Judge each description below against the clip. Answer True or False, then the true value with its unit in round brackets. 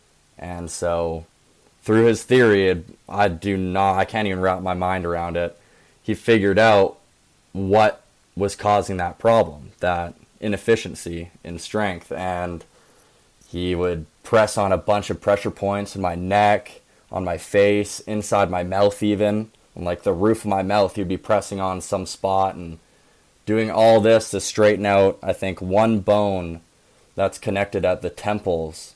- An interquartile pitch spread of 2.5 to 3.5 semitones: True (2.8 semitones)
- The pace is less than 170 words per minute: True (160 wpm)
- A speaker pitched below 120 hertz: True (100 Hz)